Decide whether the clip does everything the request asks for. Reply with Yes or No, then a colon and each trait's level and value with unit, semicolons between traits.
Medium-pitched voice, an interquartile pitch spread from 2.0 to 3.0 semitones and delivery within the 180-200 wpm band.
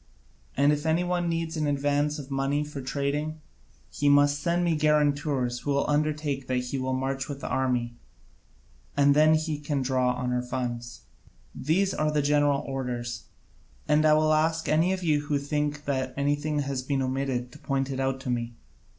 Yes: medium, 145 Hz; narrow, 2.4 semitones; average, 185 wpm